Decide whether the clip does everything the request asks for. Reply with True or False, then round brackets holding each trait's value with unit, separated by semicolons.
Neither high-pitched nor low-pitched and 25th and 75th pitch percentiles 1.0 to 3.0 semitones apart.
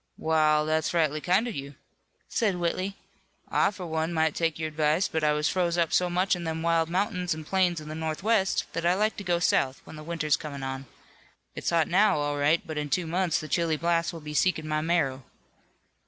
True (165 Hz; 2.6 semitones)